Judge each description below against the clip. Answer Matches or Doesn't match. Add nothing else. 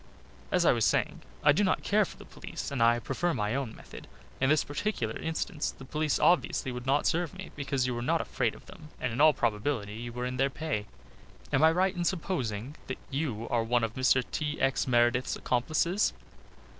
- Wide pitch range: Doesn't match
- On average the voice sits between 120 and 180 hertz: Matches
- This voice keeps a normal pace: Doesn't match